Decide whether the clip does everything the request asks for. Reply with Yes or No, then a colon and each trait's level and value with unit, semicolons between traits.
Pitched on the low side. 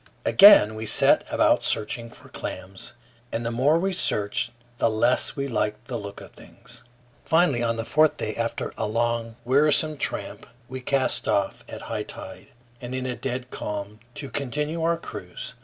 Yes: low, 120 Hz